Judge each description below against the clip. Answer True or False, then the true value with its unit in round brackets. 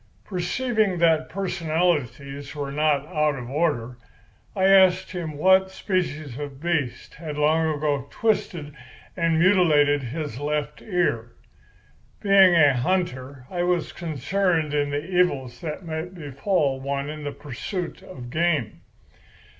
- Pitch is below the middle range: False (155 Hz)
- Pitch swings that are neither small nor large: True (4.0 semitones)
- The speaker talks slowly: True (130 wpm)